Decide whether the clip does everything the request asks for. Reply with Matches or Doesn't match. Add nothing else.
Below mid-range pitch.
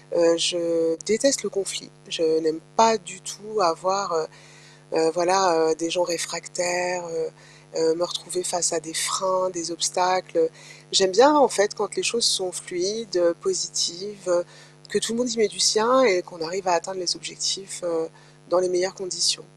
Doesn't match